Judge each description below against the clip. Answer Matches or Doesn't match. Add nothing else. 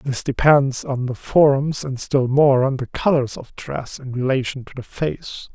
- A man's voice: Matches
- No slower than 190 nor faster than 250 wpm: Matches